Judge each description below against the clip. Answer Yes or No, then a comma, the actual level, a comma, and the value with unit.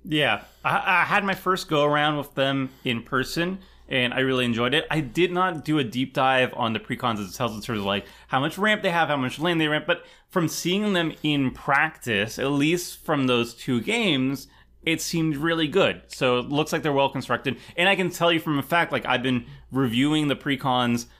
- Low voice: No, medium, 145 Hz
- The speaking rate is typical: No, fast, 230 wpm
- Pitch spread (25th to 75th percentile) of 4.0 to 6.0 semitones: Yes, average, 4.6 semitones